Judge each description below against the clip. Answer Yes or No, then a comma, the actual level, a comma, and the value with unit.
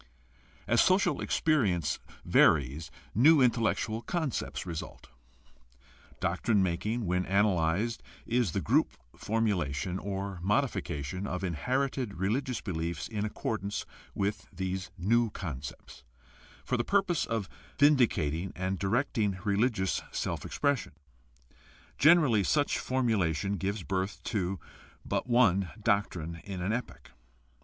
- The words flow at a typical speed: No, slow, 115 wpm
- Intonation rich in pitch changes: No, average, 4.8 semitones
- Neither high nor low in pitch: No, low, 100 Hz